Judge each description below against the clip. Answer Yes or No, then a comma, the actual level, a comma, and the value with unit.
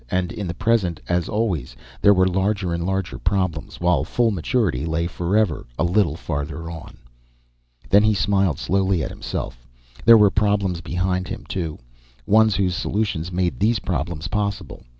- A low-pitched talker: Yes, very low, 95 Hz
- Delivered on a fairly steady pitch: No, average, 3.2 semitones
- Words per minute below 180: Yes, average, 160 wpm